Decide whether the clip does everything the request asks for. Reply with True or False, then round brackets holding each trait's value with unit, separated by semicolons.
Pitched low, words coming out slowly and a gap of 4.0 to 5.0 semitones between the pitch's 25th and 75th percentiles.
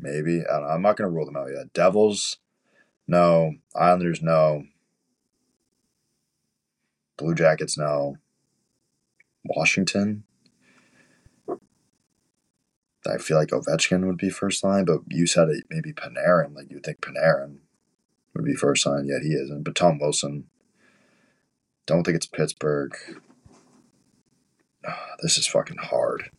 True (80 Hz; 125 wpm; 4.5 semitones)